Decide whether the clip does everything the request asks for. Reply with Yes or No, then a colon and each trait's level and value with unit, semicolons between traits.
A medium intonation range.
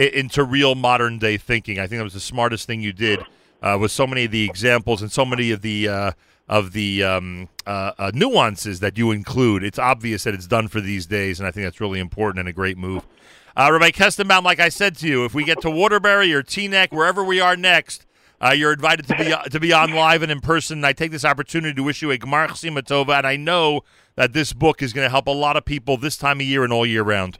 No: wide, 6.5 semitones